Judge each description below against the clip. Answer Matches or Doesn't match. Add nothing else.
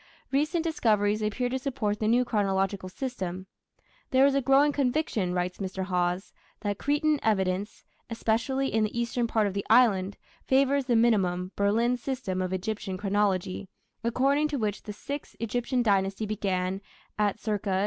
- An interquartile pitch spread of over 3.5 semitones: Matches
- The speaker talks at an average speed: Matches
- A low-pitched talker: Doesn't match